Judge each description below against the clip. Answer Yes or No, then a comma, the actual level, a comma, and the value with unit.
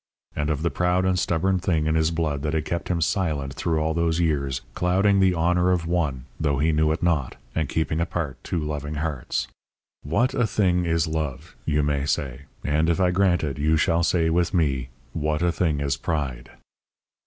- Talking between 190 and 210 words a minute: Yes, average, 200 wpm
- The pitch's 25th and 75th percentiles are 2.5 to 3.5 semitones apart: Yes, average, 2.9 semitones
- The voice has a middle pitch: No, very low, 80 Hz